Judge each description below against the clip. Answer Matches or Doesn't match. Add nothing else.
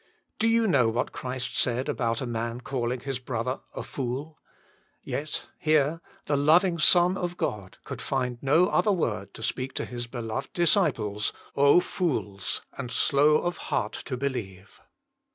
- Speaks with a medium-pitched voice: Doesn't match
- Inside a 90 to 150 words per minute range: Doesn't match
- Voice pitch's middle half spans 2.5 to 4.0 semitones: Doesn't match